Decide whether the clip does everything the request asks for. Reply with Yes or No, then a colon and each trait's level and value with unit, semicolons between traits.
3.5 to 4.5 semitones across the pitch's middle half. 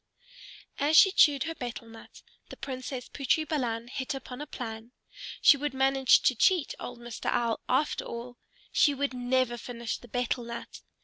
No: average, 2.7 semitones